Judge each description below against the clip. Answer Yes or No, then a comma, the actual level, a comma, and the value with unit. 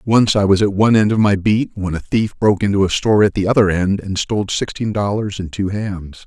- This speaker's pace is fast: Yes, fast, 260 wpm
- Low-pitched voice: Yes, low, 100 Hz